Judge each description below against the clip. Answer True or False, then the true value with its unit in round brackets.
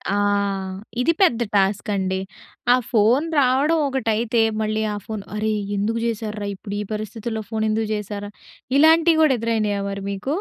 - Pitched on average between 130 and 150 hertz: False (220 Hz)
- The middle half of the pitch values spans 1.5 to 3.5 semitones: True (3.1 semitones)